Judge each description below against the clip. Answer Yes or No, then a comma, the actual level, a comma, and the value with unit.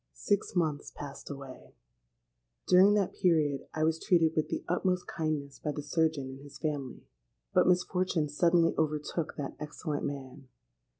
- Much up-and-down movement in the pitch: No, average, 3.3 semitones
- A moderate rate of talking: Yes, average, 145 wpm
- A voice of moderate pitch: Yes, medium, 155 Hz